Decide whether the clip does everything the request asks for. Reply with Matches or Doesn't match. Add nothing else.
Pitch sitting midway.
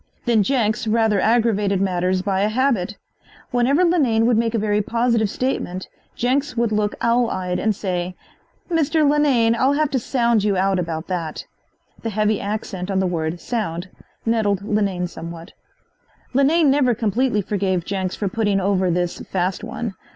Doesn't match